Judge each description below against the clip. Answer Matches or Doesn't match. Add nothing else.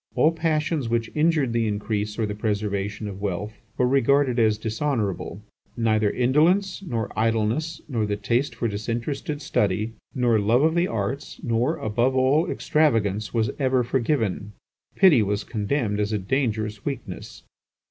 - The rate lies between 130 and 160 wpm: Matches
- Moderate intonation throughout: Matches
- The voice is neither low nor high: Doesn't match